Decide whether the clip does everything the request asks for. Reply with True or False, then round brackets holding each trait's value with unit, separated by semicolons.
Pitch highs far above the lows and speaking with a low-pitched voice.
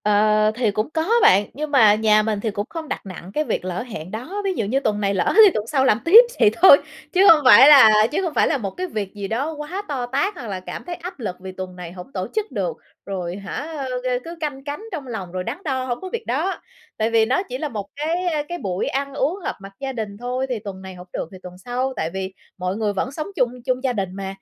False (6.9 semitones; 240 Hz)